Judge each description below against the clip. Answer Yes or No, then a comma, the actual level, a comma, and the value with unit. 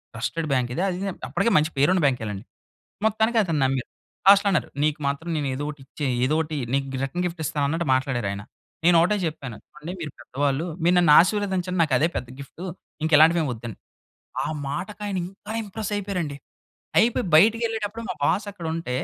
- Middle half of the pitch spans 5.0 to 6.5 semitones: Yes, wide, 5.4 semitones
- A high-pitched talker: No, medium, 165 Hz